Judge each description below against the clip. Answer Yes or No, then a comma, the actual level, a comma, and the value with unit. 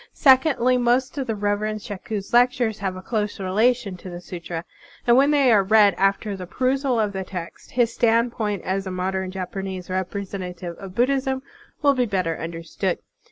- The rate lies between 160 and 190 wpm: Yes, average, 180 wpm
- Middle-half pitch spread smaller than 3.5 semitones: No, average, 4.6 semitones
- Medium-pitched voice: No, high, 205 Hz